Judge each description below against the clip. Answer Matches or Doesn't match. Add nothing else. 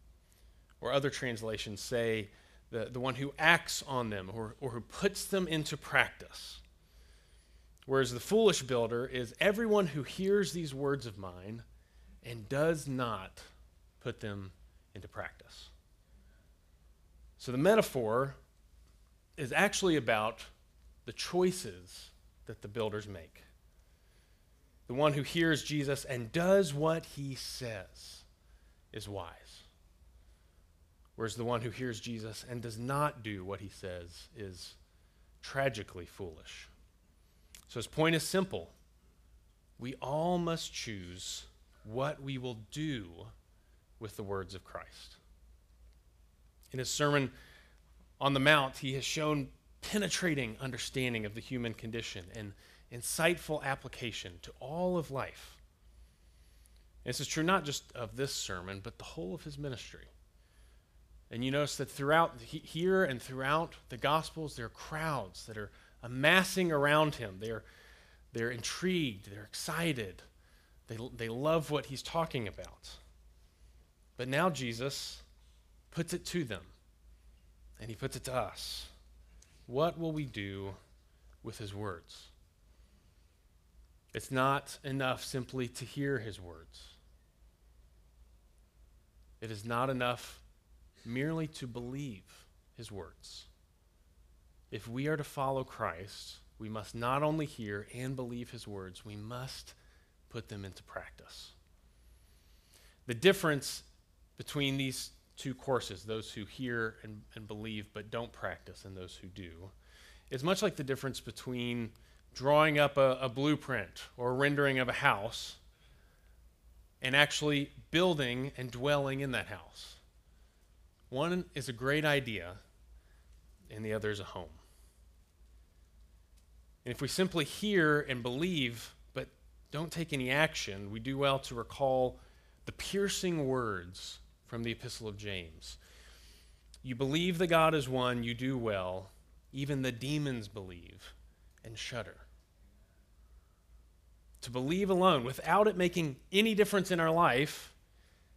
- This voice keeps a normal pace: Doesn't match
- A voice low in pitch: Matches